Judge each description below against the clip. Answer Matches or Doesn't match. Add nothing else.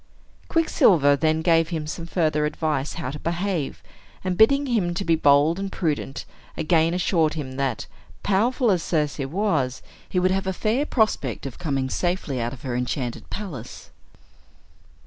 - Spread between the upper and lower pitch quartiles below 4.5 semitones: Doesn't match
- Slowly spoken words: Doesn't match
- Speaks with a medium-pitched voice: Matches